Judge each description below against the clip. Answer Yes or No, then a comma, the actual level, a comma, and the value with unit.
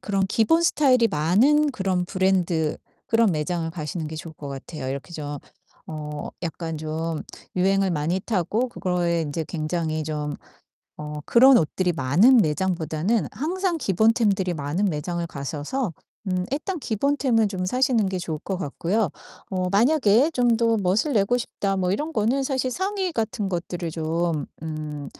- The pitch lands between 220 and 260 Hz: No, medium, 185 Hz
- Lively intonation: Yes, wide, 6.4 semitones